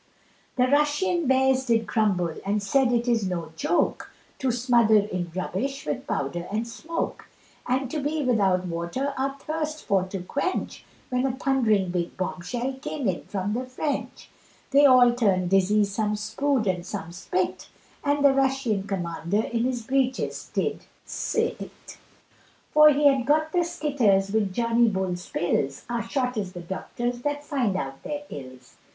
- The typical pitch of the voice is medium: No, high, 235 Hz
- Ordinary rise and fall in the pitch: No, wide, 6.2 semitones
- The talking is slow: No, average, 165 wpm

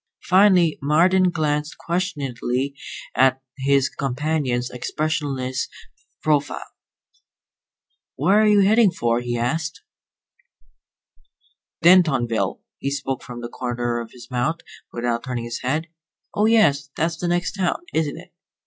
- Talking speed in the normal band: No, slow, 120 wpm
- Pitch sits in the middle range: Yes, medium, 145 Hz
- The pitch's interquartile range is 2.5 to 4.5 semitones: No, wide, 5.6 semitones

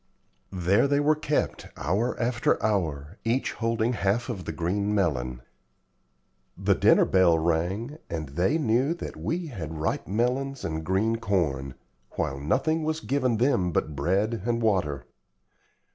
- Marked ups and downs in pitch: Yes, wide, 7.0 semitones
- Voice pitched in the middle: No, low, 105 Hz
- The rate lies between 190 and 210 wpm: No, average, 145 wpm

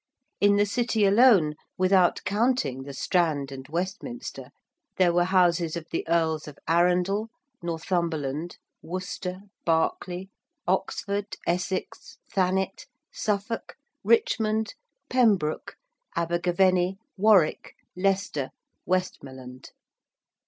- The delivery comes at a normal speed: No, slow, 90 wpm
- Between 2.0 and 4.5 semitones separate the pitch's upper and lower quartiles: Yes, average, 3.3 semitones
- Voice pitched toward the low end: No, medium, 180 Hz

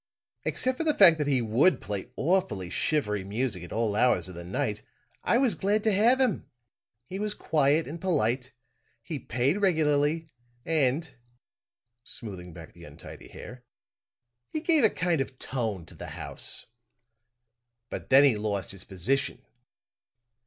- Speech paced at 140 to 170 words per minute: Yes, average, 150 wpm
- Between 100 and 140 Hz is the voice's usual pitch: Yes, low, 135 Hz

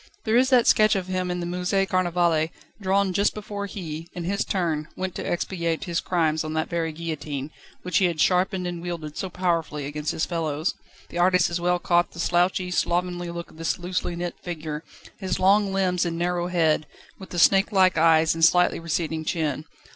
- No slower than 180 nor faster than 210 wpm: Yes, average, 195 wpm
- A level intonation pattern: Yes, narrow, 2.3 semitones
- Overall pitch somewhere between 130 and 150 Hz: No, medium, 175 Hz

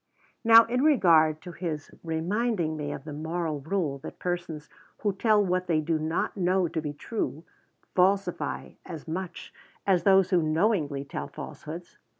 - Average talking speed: Yes, average, 155 wpm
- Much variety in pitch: No, average, 3.7 semitones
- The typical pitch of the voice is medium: Yes, medium, 170 Hz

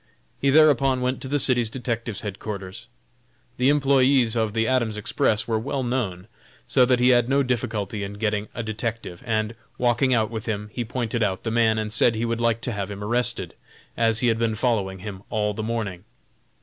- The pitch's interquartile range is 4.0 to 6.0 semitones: No, average, 2.7 semitones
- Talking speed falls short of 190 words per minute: No, average, 200 wpm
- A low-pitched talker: Yes, low, 115 Hz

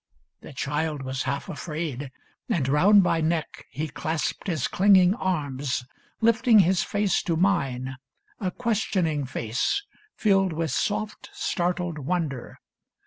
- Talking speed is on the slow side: Yes, slow, 125 wpm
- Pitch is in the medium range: Yes, medium, 165 Hz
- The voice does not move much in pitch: No, average, 5.2 semitones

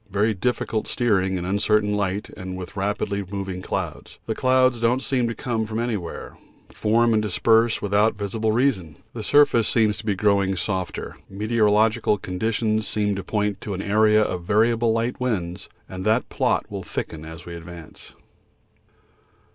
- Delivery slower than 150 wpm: No, average, 165 wpm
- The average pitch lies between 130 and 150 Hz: No, low, 105 Hz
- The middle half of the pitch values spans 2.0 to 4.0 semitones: Yes, average, 2.8 semitones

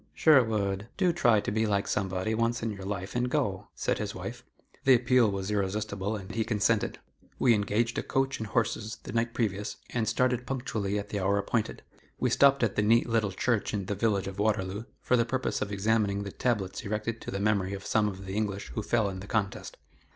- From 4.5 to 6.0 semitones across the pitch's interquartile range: No, average, 2.7 semitones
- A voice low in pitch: Yes, low, 105 Hz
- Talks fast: Yes, fast, 215 wpm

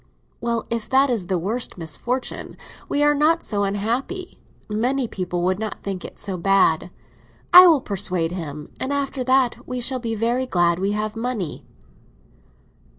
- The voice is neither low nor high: No, high, 220 Hz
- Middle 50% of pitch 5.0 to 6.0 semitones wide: Yes, wide, 5.5 semitones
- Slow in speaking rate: No, average, 160 wpm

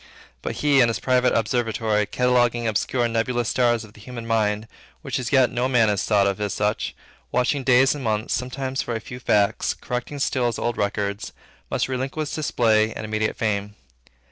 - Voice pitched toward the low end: Yes, low, 120 Hz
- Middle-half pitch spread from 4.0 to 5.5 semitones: No, average, 2.8 semitones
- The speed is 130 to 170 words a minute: No, average, 190 wpm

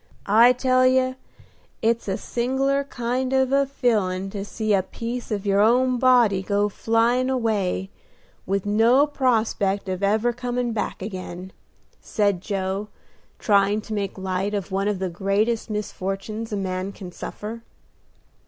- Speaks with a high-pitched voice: Yes, high, 210 Hz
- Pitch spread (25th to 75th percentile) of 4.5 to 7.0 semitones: No, average, 3.8 semitones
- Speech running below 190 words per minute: Yes, average, 145 wpm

